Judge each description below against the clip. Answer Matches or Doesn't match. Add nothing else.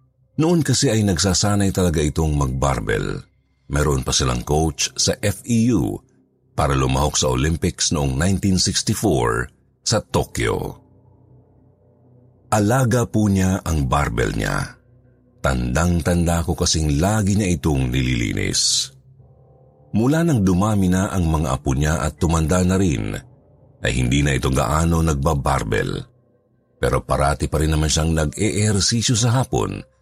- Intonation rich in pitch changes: Matches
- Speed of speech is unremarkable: Matches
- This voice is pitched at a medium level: Doesn't match